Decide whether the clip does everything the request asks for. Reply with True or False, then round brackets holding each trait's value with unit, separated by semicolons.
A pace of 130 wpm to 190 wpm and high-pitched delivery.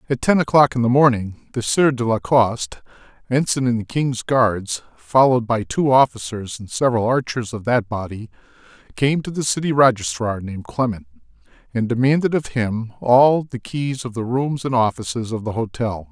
False (180 wpm; 120 Hz)